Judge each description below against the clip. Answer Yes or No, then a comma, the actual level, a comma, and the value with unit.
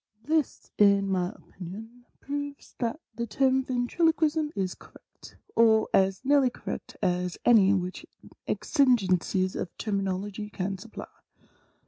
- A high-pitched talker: Yes, high, 220 Hz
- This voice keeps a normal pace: No, slow, 130 wpm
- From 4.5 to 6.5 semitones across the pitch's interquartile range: Yes, wide, 5.6 semitones